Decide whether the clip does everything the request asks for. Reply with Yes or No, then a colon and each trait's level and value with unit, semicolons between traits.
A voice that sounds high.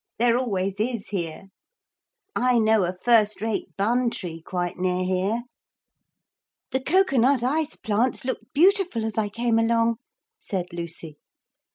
Yes: high, 225 Hz